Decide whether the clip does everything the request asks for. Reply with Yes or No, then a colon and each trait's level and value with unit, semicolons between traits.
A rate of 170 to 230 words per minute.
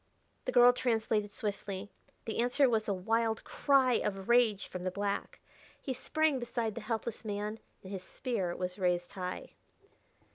No: average, 155 wpm